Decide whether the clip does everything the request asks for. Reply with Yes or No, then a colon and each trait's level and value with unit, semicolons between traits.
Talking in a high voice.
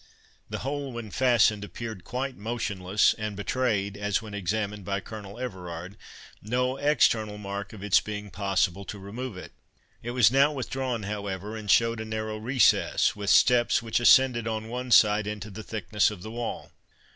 No: low, 110 Hz